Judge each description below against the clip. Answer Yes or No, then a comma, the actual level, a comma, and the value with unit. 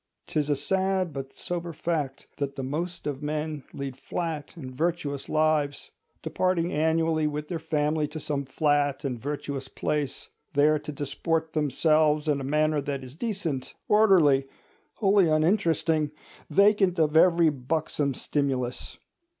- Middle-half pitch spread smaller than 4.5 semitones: Yes, narrow, 2.6 semitones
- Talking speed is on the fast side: No, average, 140 wpm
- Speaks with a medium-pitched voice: Yes, medium, 150 Hz